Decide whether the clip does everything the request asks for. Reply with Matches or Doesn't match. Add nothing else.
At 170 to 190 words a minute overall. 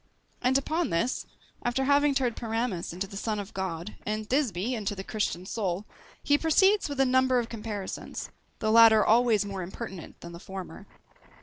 Matches